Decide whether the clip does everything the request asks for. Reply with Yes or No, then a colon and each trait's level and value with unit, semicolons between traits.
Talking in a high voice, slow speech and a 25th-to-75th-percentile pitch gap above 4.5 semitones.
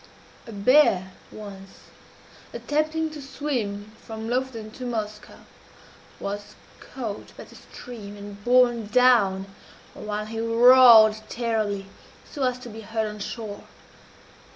No: high, 225 Hz; slow, 120 wpm; average, 3.4 semitones